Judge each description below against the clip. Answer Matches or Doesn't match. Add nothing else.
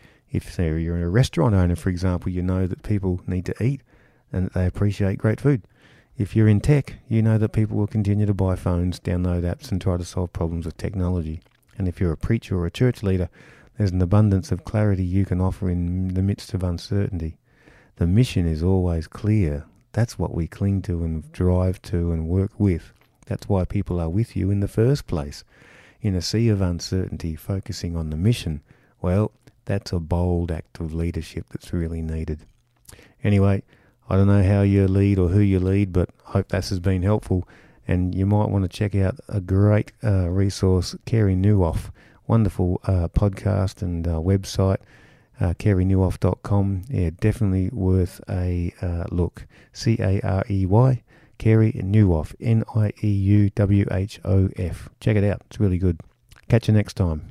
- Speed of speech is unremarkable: Matches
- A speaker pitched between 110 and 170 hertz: Doesn't match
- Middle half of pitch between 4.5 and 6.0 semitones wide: Doesn't match